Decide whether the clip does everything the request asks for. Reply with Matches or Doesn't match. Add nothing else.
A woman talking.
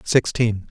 Doesn't match